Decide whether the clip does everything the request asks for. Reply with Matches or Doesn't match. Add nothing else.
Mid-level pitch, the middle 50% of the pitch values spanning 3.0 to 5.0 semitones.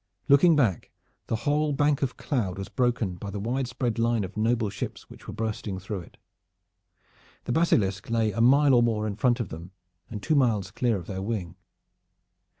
Doesn't match